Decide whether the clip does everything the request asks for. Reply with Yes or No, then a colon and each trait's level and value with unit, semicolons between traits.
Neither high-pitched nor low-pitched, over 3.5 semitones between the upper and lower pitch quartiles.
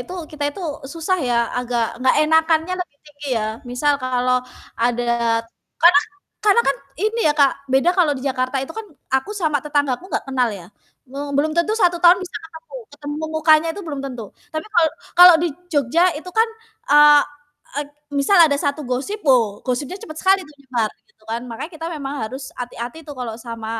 No: very high, 290 Hz; average, 4.1 semitones